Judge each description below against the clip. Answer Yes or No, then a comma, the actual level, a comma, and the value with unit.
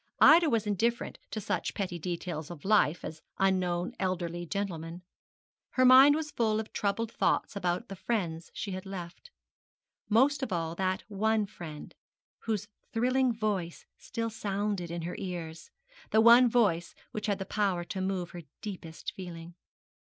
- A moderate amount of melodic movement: Yes, average, 4.1 semitones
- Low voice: No, high, 195 Hz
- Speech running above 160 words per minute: No, average, 155 wpm